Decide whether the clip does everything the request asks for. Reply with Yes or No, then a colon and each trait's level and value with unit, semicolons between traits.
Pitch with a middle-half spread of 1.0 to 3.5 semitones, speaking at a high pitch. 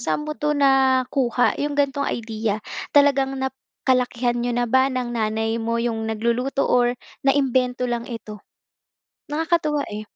Yes: average, 2.8 semitones; very high, 250 Hz